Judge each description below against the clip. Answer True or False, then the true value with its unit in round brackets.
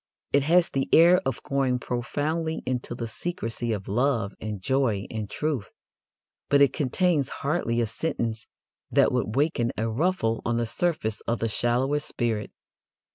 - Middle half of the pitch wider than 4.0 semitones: True (4.5 semitones)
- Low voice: True (125 Hz)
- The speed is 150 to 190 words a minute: True (155 wpm)